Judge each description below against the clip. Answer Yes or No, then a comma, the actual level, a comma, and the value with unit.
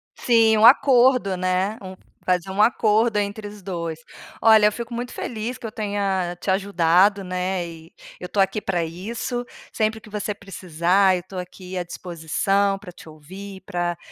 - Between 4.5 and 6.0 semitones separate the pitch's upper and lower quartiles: No, average, 3.0 semitones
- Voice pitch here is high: Yes, high, 195 Hz